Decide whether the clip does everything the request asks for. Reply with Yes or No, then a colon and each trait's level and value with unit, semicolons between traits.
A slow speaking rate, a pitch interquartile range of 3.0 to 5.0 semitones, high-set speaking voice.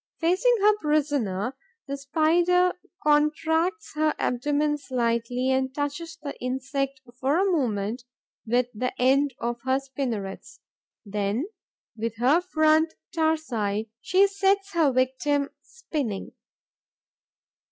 Yes: slow, 110 wpm; average, 4.4 semitones; very high, 280 Hz